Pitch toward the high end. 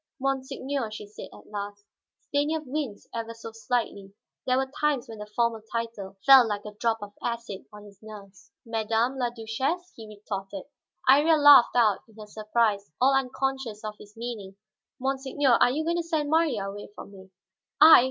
Yes: high, 230 Hz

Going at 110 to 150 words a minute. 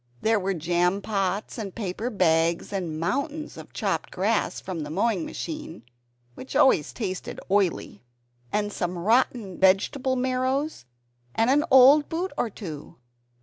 Yes: average, 140 wpm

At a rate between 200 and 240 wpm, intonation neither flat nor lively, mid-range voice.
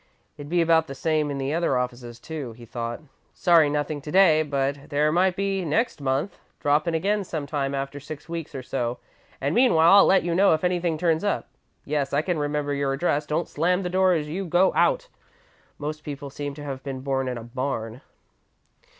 Yes: fast, 205 wpm; average, 3.7 semitones; medium, 150 Hz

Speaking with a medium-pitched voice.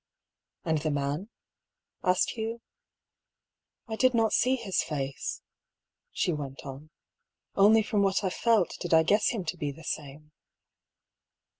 Yes: medium, 180 Hz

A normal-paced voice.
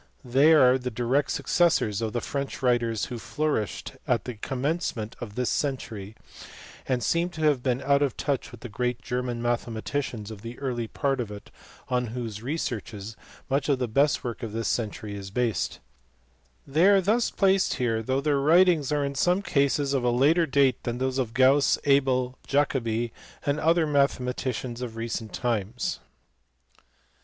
Yes: average, 170 wpm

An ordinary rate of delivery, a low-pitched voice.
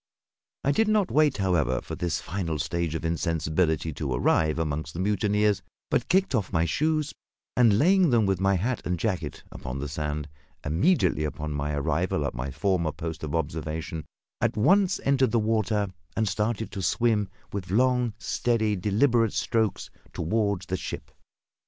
Yes: average, 165 wpm; very low, 95 Hz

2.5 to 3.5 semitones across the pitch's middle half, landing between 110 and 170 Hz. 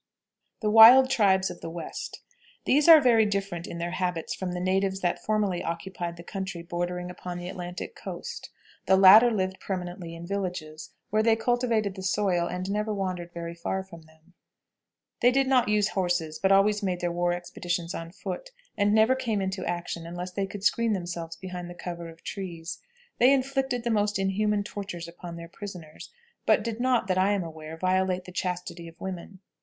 No: average, 3.2 semitones; medium, 185 Hz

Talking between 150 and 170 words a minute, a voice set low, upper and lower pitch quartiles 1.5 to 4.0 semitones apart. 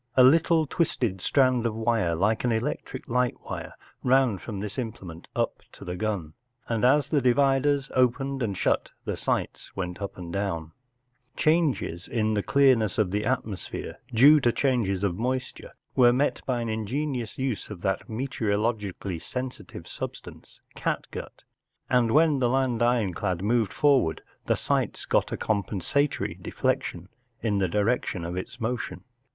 No: average, 160 wpm; low, 115 Hz; average, 4.6 semitones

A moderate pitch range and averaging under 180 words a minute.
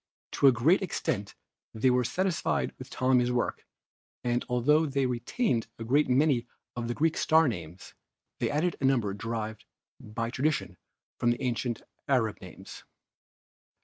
Yes: average, 3.6 semitones; average, 145 wpm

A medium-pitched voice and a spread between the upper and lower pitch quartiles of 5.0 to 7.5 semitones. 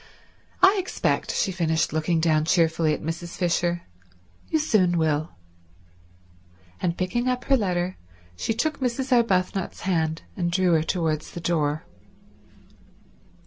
No: medium, 175 Hz; average, 3.8 semitones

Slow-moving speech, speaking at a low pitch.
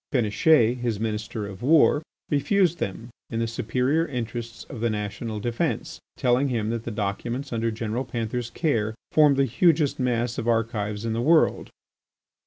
No: average, 160 wpm; low, 120 Hz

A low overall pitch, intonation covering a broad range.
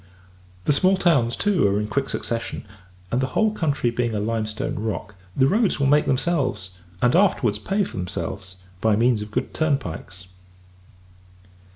Yes: low, 120 Hz; wide, 5.8 semitones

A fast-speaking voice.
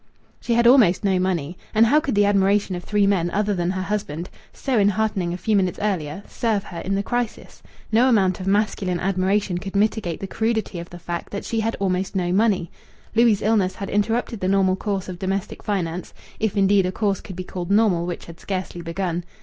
Yes: fast, 210 wpm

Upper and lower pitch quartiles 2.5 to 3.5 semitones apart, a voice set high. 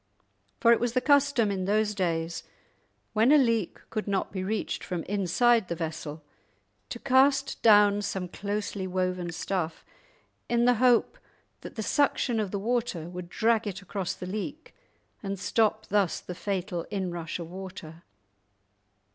No: average, 4.2 semitones; high, 200 Hz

